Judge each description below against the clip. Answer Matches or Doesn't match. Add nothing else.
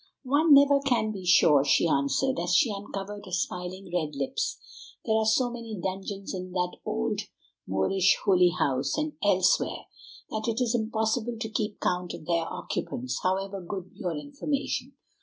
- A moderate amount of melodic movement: Matches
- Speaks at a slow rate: Doesn't match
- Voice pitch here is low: Doesn't match